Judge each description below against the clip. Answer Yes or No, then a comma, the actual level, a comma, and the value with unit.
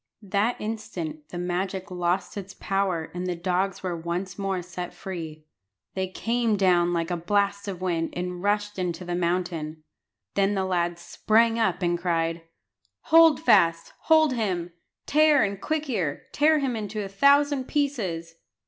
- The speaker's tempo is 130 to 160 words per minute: Yes, average, 155 wpm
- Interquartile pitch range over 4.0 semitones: No, average, 3.5 semitones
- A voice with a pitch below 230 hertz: Yes, medium, 185 Hz